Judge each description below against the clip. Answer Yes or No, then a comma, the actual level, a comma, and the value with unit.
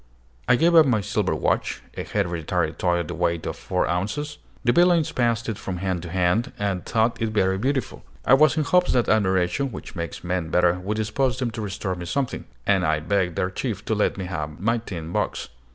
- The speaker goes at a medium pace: No, fast, 215 wpm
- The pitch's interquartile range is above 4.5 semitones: Yes, average, 5.1 semitones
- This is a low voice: Yes, low, 100 Hz